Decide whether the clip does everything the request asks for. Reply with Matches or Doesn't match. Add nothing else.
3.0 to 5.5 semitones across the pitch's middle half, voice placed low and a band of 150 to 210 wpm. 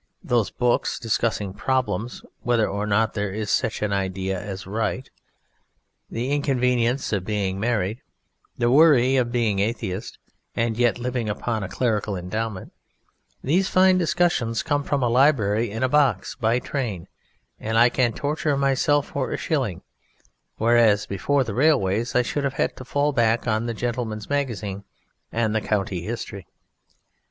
Matches